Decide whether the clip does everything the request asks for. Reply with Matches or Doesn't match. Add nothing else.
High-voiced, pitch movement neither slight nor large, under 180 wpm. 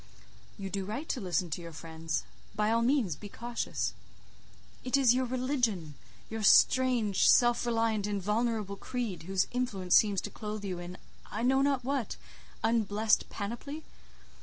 Matches